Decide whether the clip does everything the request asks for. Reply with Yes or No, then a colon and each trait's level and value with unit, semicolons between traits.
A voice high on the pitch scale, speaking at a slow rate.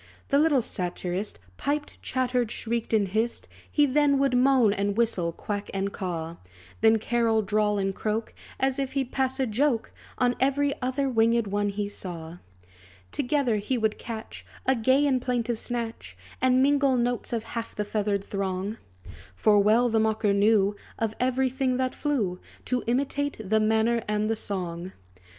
No: high, 225 Hz; average, 165 wpm